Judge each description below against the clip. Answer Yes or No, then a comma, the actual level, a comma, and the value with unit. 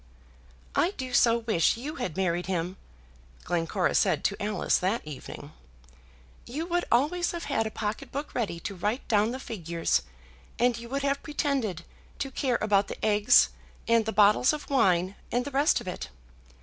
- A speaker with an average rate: Yes, average, 175 wpm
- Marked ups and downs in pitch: Yes, wide, 5.8 semitones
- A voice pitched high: Yes, high, 225 Hz